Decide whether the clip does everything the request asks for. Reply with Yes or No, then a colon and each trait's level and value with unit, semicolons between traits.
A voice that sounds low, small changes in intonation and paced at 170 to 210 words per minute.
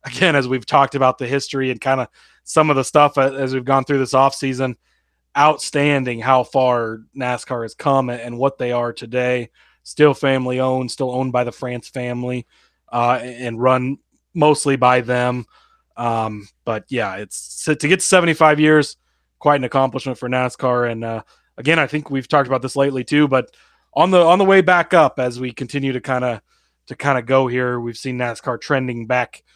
Yes: low, 130 Hz; narrow, 2.2 semitones; average, 195 wpm